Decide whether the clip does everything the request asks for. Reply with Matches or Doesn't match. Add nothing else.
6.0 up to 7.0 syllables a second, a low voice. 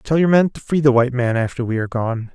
Matches